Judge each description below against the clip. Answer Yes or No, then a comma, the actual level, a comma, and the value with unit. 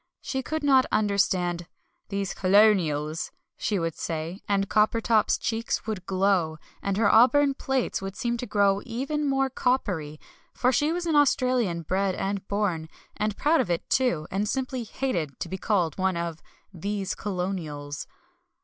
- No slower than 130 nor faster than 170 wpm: Yes, average, 155 wpm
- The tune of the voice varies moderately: No, wide, 5.9 semitones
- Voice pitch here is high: Yes, high, 200 Hz